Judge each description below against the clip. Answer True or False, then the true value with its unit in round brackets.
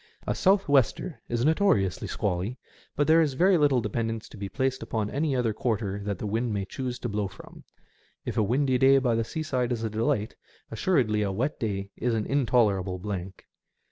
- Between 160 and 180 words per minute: False (195 wpm)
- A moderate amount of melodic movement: True (4.5 semitones)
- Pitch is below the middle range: True (115 Hz)